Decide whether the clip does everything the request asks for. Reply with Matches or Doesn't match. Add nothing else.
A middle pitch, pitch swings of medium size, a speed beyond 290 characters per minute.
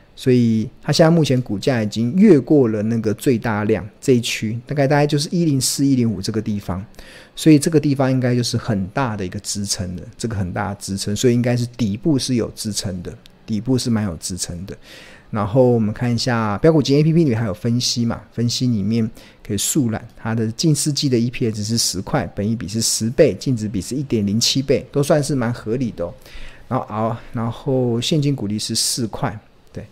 Doesn't match